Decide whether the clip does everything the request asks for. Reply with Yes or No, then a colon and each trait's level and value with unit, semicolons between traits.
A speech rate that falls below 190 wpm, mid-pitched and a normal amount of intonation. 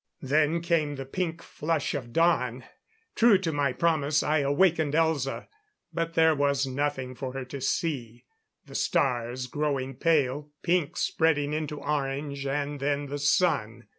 Yes: average, 145 wpm; medium, 145 Hz; average, 3.0 semitones